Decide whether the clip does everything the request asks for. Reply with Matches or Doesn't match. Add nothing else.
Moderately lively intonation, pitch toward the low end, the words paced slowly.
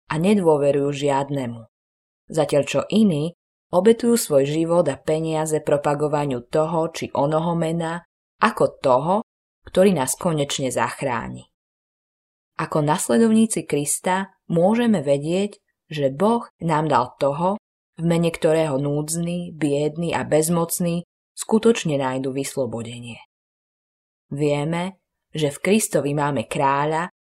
Doesn't match